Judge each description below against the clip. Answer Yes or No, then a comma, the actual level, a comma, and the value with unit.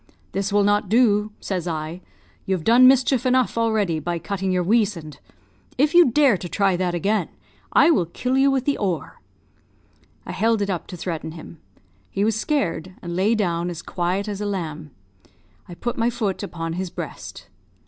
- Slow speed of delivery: No, average, 180 wpm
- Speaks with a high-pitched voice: Yes, high, 200 Hz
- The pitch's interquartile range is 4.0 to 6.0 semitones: Yes, average, 4.8 semitones